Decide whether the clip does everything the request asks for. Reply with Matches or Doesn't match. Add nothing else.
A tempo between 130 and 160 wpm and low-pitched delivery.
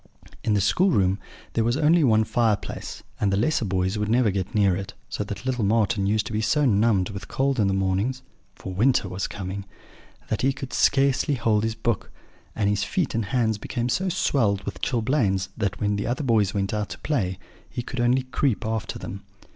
Doesn't match